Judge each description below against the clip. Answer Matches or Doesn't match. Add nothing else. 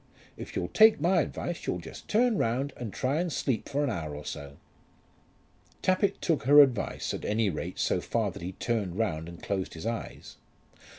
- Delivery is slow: Doesn't match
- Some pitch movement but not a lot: Doesn't match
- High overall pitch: Doesn't match